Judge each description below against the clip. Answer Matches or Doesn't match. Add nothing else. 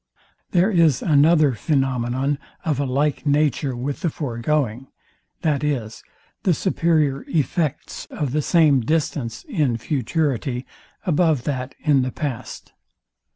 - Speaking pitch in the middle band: Matches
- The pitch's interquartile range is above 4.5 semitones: Doesn't match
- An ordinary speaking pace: Doesn't match